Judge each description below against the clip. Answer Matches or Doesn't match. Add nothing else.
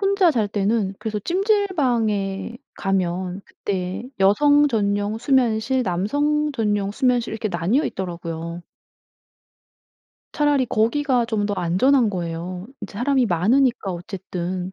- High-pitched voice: Matches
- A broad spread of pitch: Matches